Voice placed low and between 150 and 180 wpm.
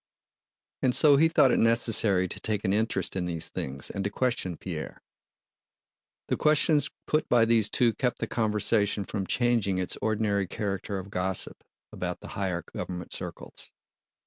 Yes: low, 105 Hz; average, 160 wpm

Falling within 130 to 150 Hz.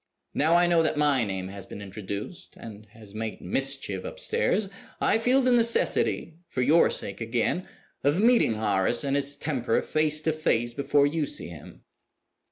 Yes: medium, 140 Hz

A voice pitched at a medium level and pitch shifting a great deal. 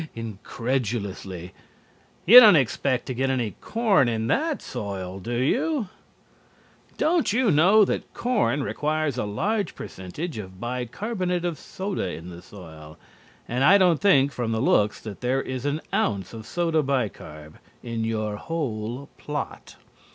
No: low, 130 Hz; wide, 8.6 semitones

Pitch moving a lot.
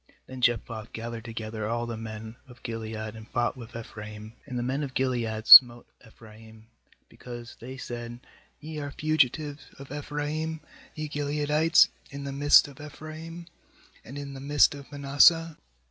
No: average, 4.3 semitones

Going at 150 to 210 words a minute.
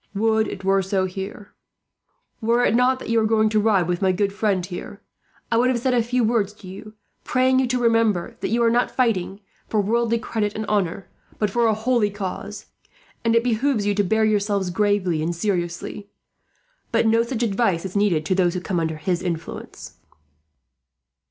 Yes: average, 195 wpm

